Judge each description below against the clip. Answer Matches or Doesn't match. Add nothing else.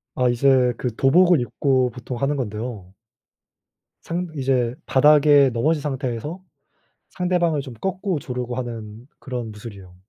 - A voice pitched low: Matches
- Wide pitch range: Doesn't match